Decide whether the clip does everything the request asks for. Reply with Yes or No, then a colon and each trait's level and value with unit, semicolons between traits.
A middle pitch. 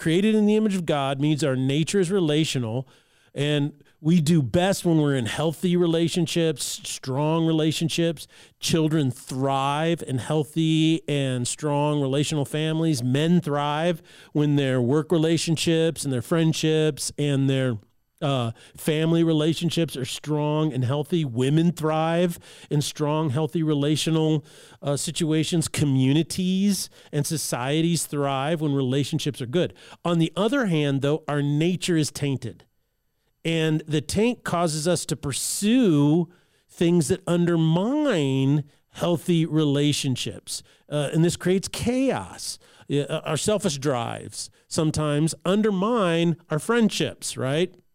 Yes: medium, 155 Hz